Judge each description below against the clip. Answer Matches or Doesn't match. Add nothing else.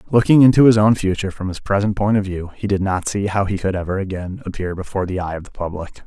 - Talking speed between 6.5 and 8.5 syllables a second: Matches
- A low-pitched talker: Matches